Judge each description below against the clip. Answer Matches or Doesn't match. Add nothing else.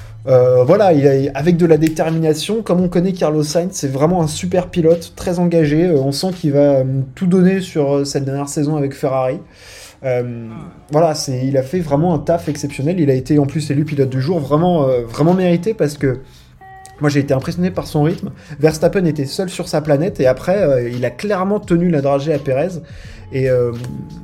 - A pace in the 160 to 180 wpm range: Doesn't match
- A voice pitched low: Doesn't match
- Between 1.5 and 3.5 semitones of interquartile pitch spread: Doesn't match